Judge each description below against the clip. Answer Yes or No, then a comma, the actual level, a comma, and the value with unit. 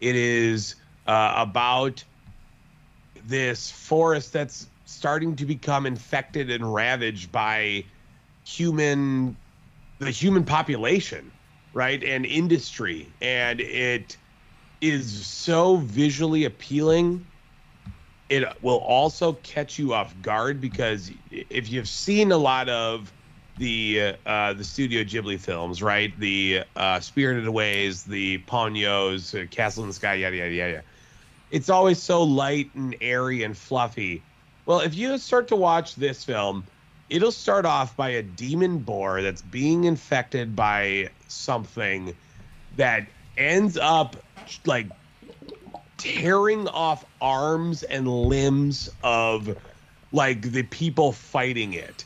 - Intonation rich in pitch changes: Yes, wide, 5.9 semitones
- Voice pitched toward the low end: Yes, low, 130 Hz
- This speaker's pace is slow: Yes, slow, 120 wpm